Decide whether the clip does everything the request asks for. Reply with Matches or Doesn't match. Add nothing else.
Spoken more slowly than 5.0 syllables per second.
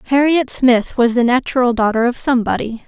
Doesn't match